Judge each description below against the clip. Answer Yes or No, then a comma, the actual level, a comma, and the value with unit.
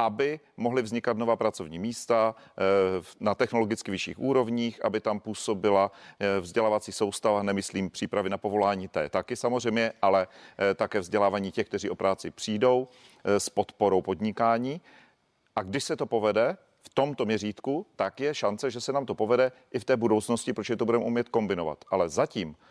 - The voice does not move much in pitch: No, average, 3.3 semitones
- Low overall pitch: Yes, low, 110 Hz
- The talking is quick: No, average, 160 wpm